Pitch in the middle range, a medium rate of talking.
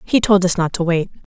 No: medium, 180 Hz; fast, 275 wpm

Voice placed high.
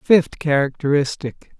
No: medium, 145 Hz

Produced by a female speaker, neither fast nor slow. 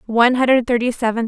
Yes: female; average, 190 wpm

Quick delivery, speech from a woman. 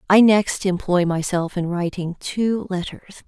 No: average, 145 wpm; female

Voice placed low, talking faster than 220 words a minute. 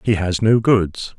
No: low, 100 Hz; average, 200 wpm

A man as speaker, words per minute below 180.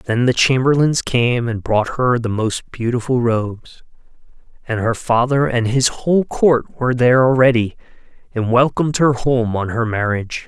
Yes: male; average, 160 wpm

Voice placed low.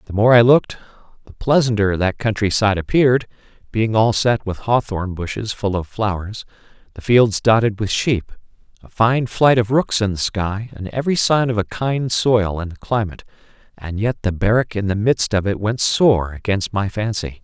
Yes: low, 110 Hz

